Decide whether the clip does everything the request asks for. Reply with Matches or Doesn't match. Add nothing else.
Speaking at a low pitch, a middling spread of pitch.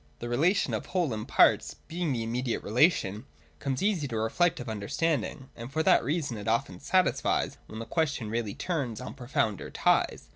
Doesn't match